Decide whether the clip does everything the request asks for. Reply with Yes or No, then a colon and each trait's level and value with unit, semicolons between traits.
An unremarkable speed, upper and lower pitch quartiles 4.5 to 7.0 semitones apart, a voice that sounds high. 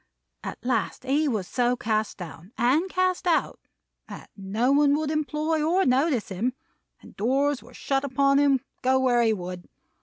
Yes: average, 170 wpm; average, 4.8 semitones; very high, 260 Hz